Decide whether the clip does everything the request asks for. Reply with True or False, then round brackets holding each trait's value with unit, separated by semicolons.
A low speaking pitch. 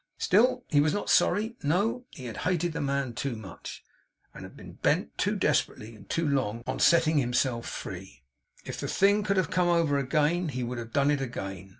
False (145 Hz)